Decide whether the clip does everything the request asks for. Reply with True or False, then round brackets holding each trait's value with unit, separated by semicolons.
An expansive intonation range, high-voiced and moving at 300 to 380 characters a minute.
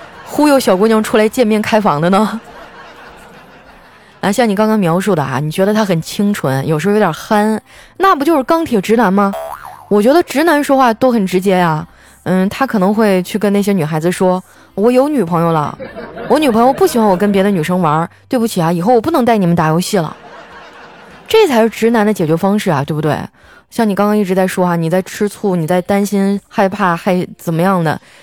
False (4.0 semitones; 200 Hz; 305 characters per minute)